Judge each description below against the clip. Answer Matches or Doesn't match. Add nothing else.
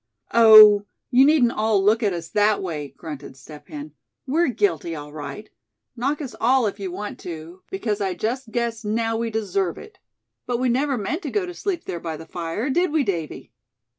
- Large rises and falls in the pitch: Matches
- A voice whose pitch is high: Matches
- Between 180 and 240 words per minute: Matches